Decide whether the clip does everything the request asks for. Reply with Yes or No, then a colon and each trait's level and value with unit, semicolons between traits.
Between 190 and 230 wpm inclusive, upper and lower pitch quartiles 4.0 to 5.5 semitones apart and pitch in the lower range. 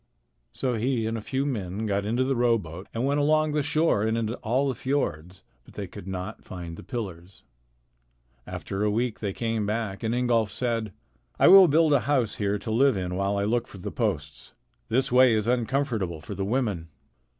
Yes: average, 200 wpm; average, 4.5 semitones; low, 115 Hz